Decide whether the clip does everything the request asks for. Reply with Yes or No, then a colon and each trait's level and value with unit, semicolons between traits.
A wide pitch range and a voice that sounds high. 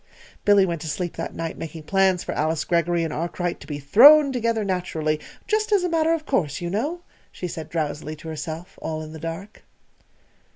No: wide, 5.7 semitones; medium, 175 Hz